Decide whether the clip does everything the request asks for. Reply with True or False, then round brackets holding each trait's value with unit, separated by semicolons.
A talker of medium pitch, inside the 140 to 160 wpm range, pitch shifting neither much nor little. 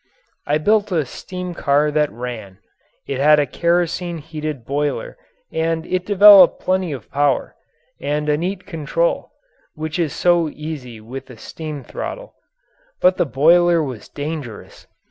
True (155 Hz; 145 wpm; 3.7 semitones)